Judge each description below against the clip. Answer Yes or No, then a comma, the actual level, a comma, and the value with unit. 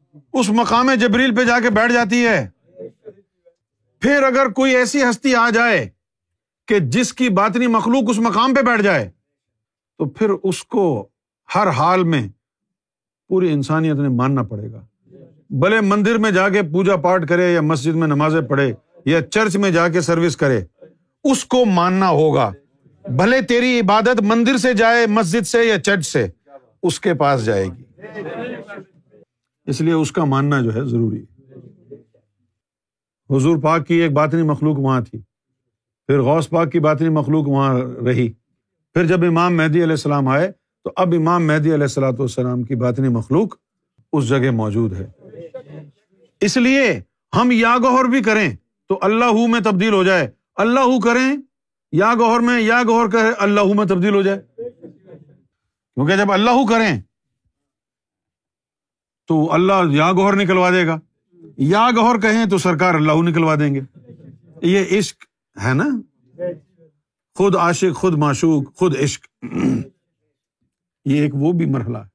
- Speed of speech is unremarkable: Yes, average, 155 wpm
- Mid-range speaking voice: Yes, medium, 170 Hz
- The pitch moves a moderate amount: No, wide, 7.7 semitones